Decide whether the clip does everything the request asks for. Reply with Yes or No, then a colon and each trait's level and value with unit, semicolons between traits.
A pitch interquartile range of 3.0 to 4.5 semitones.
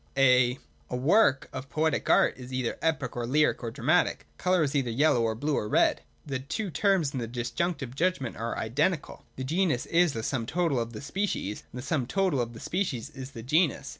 No: average, 5.0 semitones